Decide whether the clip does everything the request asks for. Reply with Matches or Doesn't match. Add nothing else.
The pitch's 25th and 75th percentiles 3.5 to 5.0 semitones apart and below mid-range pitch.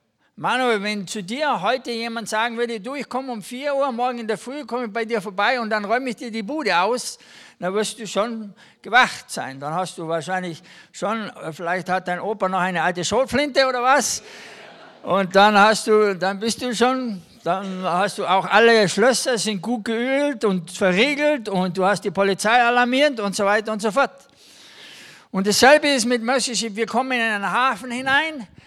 Doesn't match